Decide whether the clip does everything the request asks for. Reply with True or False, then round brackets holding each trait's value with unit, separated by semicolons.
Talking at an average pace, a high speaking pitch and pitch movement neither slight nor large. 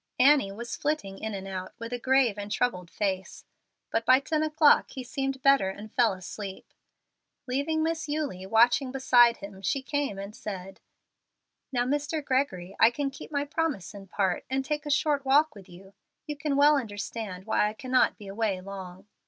False (185 wpm; 240 Hz; 6.3 semitones)